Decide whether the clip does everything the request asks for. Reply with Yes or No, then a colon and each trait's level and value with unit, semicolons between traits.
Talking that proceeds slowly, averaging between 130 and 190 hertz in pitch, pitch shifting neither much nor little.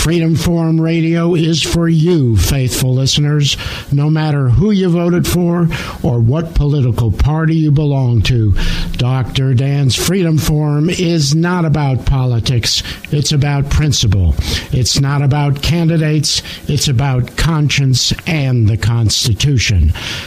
Yes: slow, 125 wpm; medium, 140 Hz; average, 4.9 semitones